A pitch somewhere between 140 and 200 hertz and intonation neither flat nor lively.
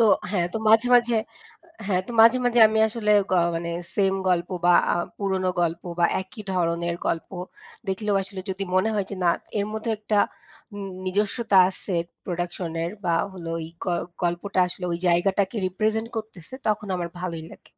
Yes: high, 190 Hz; average, 3.5 semitones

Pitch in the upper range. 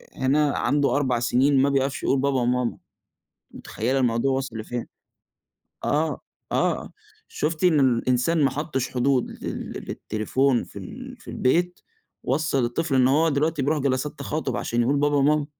No: low, 135 Hz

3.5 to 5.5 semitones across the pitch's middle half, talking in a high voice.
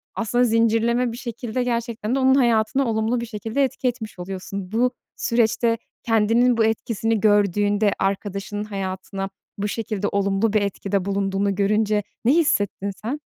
No: average, 2.8 semitones; high, 220 Hz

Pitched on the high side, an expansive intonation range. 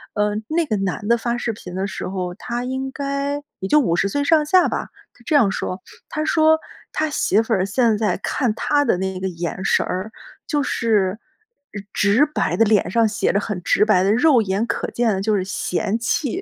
Yes: high, 220 Hz; wide, 6.3 semitones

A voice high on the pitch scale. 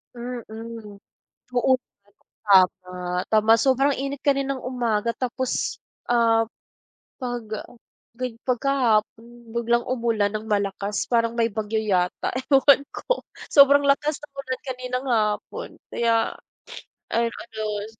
Yes: high, 235 Hz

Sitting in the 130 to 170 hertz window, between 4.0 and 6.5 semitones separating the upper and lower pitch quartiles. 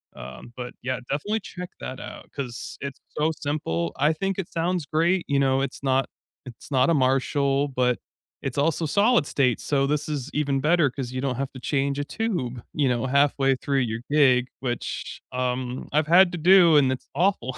No: medium, 140 Hz; average, 3.3 semitones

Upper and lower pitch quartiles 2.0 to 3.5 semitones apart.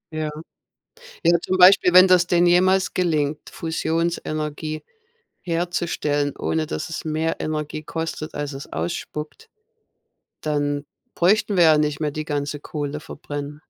Yes: average, 2.7 semitones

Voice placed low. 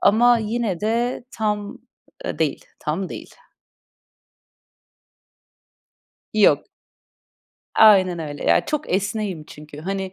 No: high, 200 Hz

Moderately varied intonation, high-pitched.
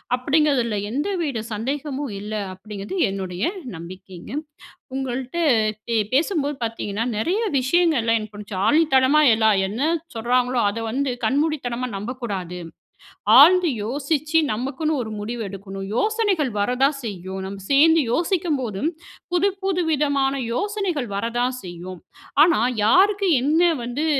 No: wide, 6.2 semitones; very high, 255 Hz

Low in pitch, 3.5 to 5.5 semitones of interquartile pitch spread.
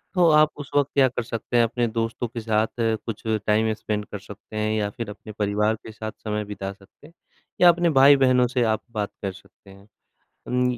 No: low, 110 Hz; average, 3.1 semitones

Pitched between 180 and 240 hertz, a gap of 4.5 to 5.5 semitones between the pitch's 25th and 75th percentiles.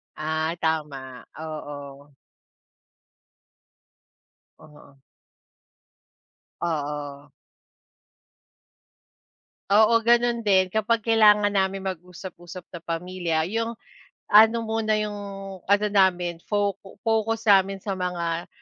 Yes: medium, 185 Hz; average, 4.9 semitones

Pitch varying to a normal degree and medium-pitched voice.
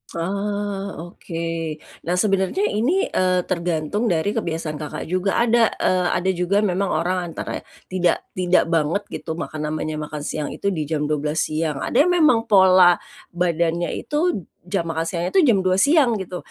Yes: average, 3.6 semitones; medium, 180 Hz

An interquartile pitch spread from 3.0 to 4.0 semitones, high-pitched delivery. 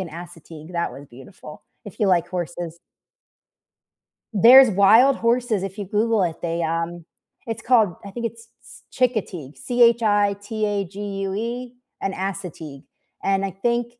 No: average, 4.9 semitones; high, 195 Hz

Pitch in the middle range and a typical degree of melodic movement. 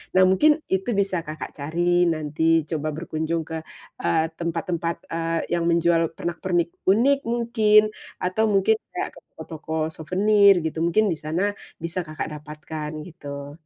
Yes: medium, 170 Hz; average, 3.3 semitones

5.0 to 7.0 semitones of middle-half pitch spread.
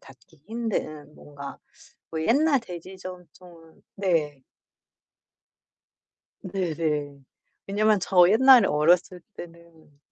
No: average, 4.3 semitones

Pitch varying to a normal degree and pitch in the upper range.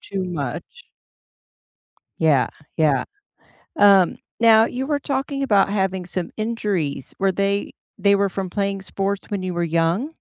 Yes: average, 3.3 semitones; high, 195 Hz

